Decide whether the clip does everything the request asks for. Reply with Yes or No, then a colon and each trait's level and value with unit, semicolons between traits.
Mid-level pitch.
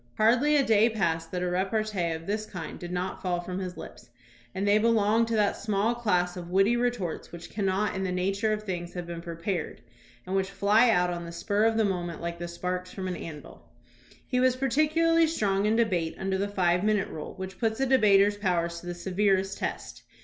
No: high, 195 Hz